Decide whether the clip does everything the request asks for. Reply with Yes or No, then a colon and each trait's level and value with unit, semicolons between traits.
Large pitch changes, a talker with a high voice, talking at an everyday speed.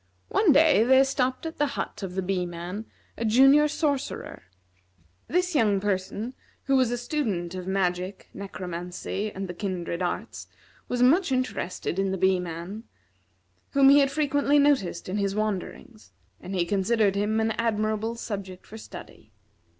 Yes: wide, 5.9 semitones; high, 210 Hz; average, 160 wpm